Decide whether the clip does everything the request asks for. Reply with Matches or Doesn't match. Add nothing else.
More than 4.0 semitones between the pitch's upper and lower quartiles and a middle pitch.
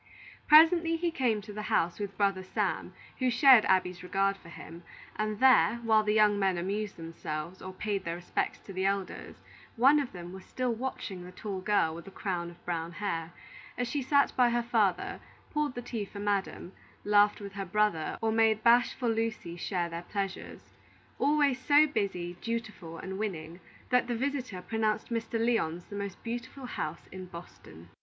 Doesn't match